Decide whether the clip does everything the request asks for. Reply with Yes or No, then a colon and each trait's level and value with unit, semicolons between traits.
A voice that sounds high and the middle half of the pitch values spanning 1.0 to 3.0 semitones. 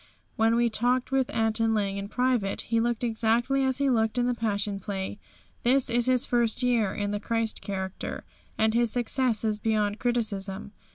Yes: high, 225 Hz; average, 2.7 semitones